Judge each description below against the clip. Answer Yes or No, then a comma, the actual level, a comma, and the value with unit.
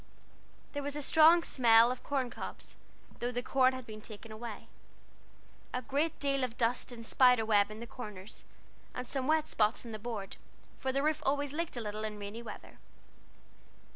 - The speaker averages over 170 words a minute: Yes, average, 180 wpm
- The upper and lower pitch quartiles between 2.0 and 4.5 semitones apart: Yes, average, 4.0 semitones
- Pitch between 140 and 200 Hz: No, high, 245 Hz